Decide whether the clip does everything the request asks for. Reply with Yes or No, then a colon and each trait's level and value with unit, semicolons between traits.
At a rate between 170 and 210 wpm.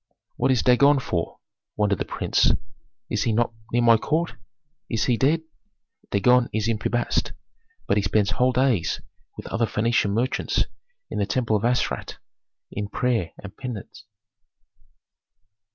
No: average, 150 wpm